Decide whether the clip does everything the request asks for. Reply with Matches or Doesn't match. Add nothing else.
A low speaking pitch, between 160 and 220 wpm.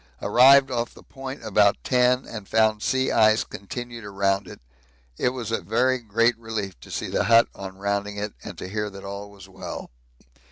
Matches